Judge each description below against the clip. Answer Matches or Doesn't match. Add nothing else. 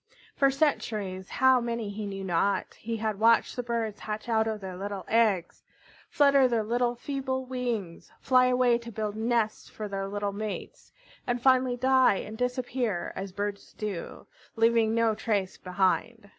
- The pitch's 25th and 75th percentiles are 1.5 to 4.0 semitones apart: Matches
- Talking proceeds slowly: Doesn't match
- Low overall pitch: Doesn't match